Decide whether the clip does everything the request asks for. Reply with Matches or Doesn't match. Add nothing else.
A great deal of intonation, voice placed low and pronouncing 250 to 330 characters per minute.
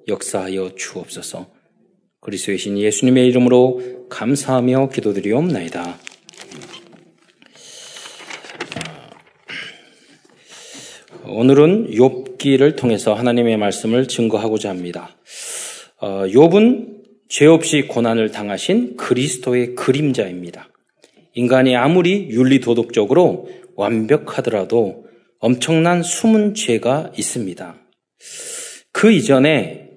Doesn't match